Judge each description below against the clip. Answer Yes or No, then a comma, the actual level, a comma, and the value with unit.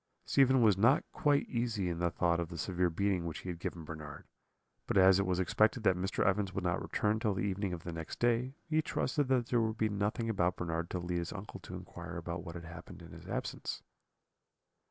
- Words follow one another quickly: Yes, fast, 230 wpm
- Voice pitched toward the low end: Yes, very low, 95 Hz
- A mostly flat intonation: No, average, 4.3 semitones